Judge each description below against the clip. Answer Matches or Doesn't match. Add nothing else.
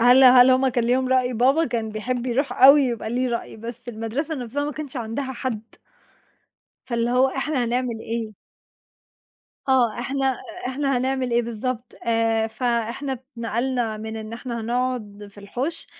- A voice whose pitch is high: Matches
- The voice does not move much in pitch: Matches